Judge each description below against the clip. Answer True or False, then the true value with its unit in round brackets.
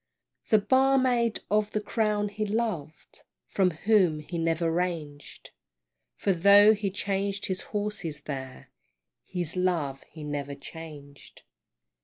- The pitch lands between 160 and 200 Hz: True (185 Hz)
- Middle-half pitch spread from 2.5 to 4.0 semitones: False (5.1 semitones)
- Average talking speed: False (120 wpm)